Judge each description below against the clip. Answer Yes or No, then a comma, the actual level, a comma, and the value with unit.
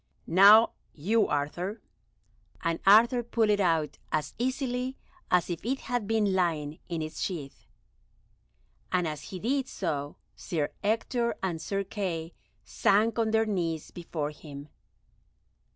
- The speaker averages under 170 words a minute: Yes, slow, 135 wpm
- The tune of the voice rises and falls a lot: Yes, wide, 5.8 semitones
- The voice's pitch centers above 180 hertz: Yes, high, 190 Hz